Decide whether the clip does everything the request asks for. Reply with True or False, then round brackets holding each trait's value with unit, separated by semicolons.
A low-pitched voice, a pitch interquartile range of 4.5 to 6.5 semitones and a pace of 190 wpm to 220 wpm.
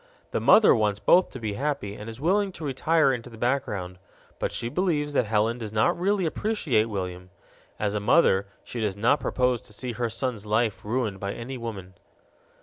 True (115 Hz; 5.1 semitones; 195 wpm)